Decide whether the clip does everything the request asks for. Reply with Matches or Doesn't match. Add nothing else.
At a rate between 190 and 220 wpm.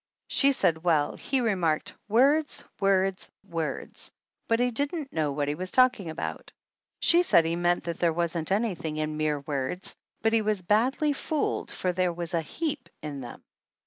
Doesn't match